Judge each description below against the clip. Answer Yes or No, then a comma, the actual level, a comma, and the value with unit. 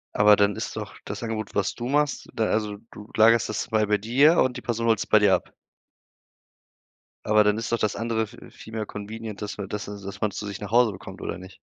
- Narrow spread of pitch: Yes, narrow, 1.9 semitones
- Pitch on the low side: Yes, low, 110 Hz